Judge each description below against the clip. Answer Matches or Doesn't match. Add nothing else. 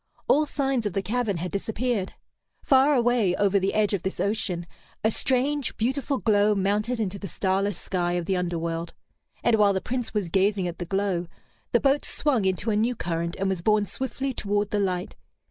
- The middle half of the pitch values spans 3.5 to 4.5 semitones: Matches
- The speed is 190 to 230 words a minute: Matches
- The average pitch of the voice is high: Matches